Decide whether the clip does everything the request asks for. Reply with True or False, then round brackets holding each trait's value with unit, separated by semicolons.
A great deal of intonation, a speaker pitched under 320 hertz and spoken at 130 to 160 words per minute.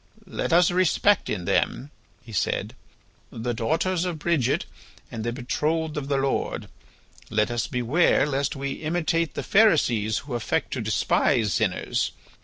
True (5.8 semitones; 140 Hz; 145 wpm)